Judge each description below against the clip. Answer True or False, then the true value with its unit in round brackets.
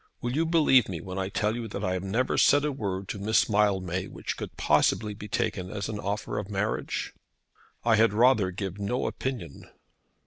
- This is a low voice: True (105 Hz)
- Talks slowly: False (200 wpm)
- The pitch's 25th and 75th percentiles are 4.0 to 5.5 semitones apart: False (3.3 semitones)